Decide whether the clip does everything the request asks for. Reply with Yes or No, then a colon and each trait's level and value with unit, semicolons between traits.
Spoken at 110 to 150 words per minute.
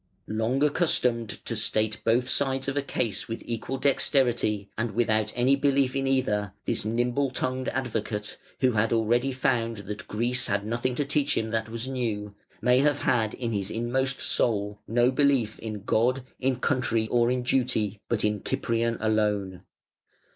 No: average, 165 wpm